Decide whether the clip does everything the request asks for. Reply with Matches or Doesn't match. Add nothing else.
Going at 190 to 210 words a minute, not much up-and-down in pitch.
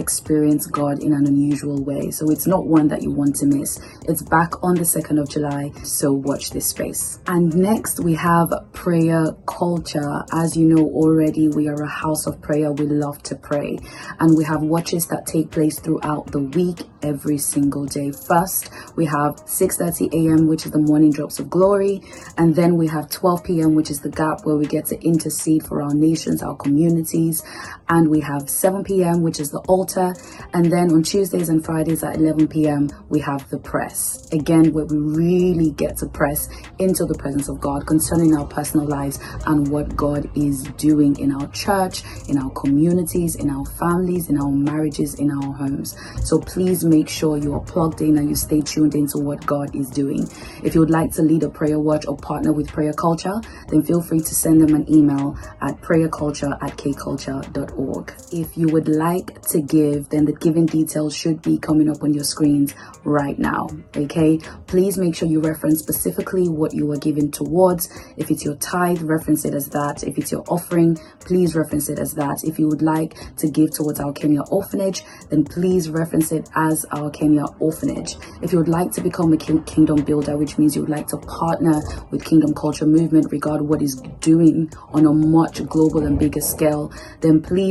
Matches